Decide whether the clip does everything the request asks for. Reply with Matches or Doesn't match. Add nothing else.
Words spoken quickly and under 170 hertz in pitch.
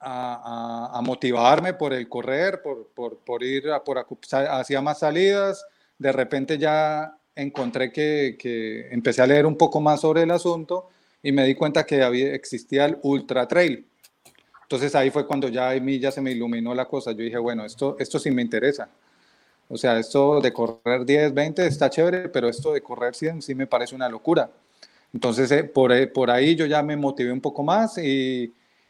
Matches